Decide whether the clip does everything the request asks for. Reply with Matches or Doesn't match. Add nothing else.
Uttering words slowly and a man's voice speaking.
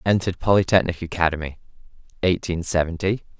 Matches